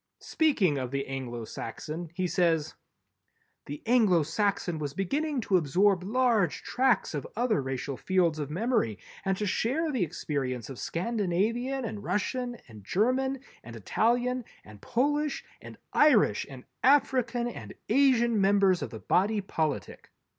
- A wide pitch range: Yes, wide, 8.3 semitones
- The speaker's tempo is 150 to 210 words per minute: No, average, 140 wpm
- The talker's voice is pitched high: Yes, high, 195 Hz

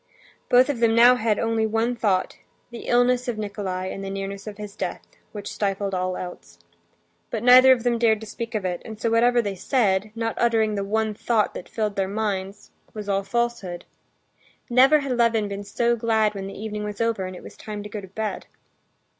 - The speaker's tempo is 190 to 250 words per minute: Yes, average, 195 wpm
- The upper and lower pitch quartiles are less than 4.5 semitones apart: Yes, average, 2.8 semitones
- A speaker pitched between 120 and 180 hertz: No, high, 215 Hz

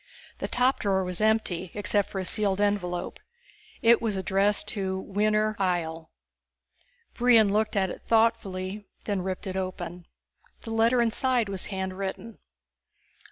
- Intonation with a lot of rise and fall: No, average, 2.7 semitones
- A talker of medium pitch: No, high, 200 Hz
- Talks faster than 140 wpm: No, slow, 135 wpm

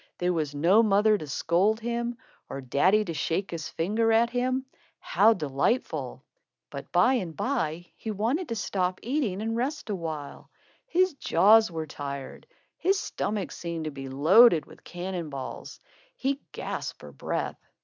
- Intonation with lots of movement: Yes, wide, 6.5 semitones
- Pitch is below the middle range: No, high, 195 Hz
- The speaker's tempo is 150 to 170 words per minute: Yes, average, 160 wpm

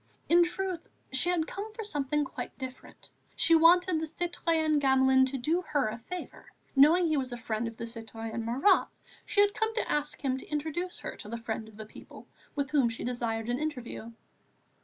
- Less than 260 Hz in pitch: No, very high, 285 Hz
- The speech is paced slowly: No, average, 200 wpm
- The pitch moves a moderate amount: No, wide, 6.0 semitones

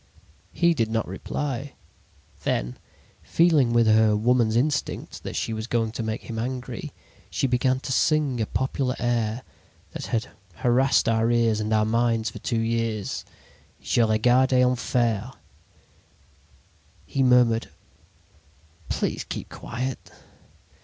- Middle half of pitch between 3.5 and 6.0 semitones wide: No, narrow, 2.5 semitones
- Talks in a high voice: No, low, 120 Hz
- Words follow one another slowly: Yes, slow, 130 wpm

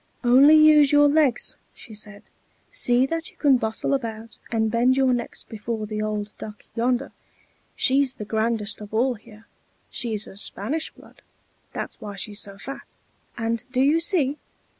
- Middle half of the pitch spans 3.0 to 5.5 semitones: Yes, average, 4.1 semitones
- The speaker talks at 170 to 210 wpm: No, average, 160 wpm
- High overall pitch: Yes, high, 235 Hz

